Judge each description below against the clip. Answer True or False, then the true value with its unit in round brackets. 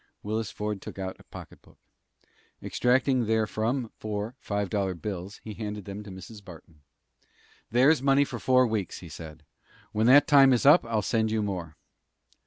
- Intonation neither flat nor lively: True (3.9 semitones)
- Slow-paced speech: False (165 wpm)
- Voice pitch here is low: True (110 Hz)